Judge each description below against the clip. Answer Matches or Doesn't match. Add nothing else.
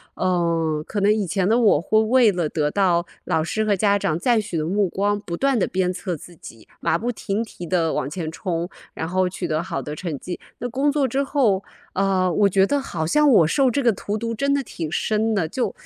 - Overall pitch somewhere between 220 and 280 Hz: Doesn't match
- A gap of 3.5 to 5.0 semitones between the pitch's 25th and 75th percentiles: Matches